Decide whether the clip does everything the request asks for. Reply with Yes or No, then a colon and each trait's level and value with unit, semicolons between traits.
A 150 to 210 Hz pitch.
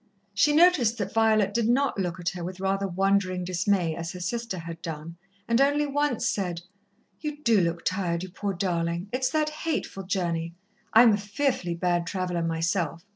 Yes: high, 190 Hz